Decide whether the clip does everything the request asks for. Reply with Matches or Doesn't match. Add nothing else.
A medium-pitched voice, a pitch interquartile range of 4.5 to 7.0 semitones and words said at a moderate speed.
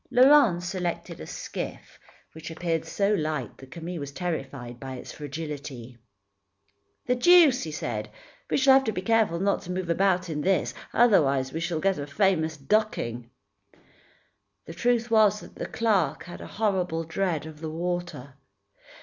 Matches